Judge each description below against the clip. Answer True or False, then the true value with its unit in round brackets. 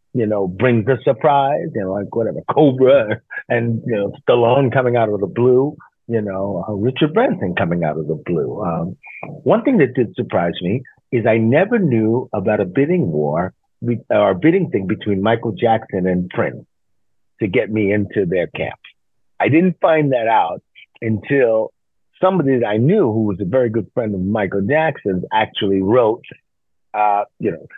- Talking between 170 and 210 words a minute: True (180 wpm)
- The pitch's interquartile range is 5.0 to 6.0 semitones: False (4.3 semitones)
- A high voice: False (115 Hz)